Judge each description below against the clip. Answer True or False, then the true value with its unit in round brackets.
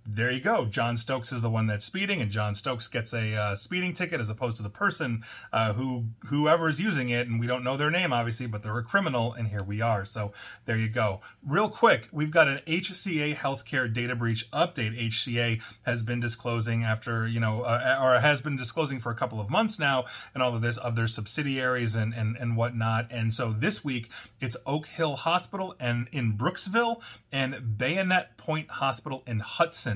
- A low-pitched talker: True (120 Hz)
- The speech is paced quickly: True (210 wpm)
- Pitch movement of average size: True (4.3 semitones)